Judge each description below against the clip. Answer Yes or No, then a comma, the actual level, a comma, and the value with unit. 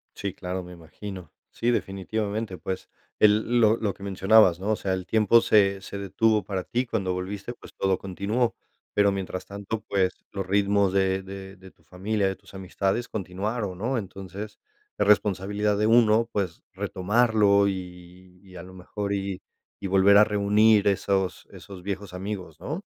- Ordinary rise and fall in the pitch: No, narrow, 2.0 semitones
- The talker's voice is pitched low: Yes, low, 100 Hz